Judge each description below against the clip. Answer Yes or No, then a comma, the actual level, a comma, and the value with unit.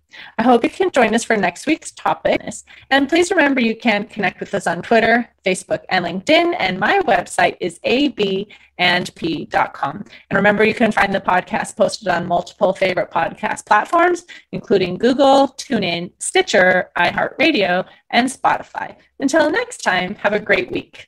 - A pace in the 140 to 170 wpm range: Yes, average, 155 wpm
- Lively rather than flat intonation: Yes, wide, 6.9 semitones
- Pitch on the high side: Yes, high, 215 Hz